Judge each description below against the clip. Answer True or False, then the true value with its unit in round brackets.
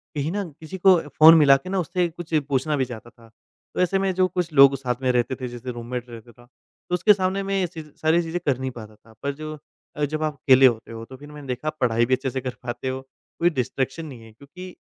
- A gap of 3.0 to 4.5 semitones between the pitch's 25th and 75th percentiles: False (4.9 semitones)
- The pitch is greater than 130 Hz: True (140 Hz)